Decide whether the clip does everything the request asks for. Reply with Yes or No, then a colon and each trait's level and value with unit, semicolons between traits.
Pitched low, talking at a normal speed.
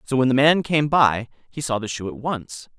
No: low, 130 Hz; fast, 260 wpm